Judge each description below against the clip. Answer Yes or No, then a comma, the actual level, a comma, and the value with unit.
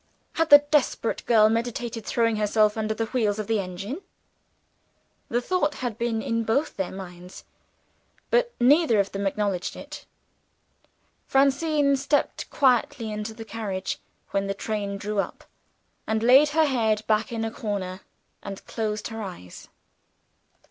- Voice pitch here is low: No, high, 220 Hz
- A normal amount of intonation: Yes, average, 3.6 semitones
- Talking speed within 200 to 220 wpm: No, average, 145 wpm